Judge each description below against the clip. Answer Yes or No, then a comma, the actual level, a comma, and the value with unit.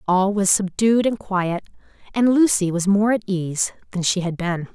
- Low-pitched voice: No, high, 195 Hz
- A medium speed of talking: Yes, average, 190 wpm